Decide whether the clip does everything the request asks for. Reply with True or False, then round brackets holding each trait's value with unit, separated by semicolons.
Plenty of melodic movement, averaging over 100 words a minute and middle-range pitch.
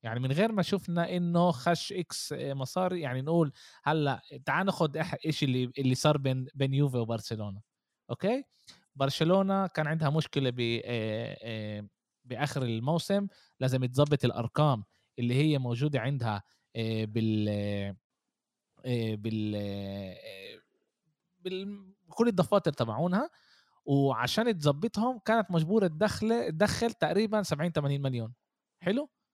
True (7.2 semitones; 110 wpm; 145 Hz)